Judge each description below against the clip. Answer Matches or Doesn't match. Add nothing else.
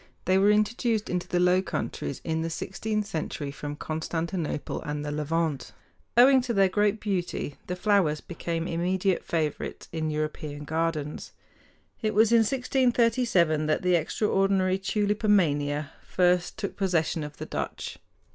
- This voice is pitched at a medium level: Matches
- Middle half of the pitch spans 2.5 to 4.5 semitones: Doesn't match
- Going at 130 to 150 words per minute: Matches